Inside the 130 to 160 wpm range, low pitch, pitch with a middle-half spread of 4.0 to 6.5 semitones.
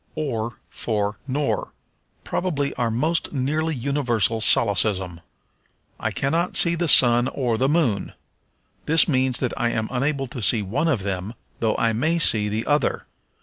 Yes: average, 150 wpm; low, 125 Hz; average, 4.9 semitones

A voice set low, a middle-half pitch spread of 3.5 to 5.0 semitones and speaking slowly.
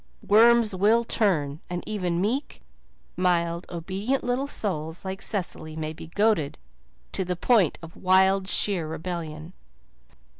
No: medium, 185 Hz; average, 4.1 semitones; slow, 125 wpm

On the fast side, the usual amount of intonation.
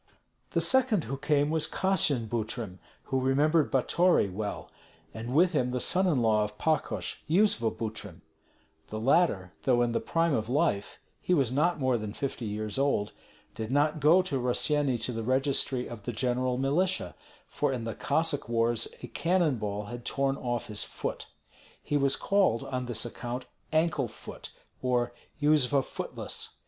No: average, 165 wpm; average, 4.7 semitones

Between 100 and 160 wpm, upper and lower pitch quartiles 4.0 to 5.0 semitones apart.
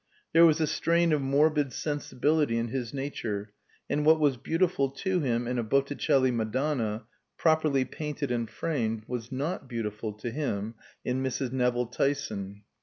Yes: average, 155 wpm; average, 4.3 semitones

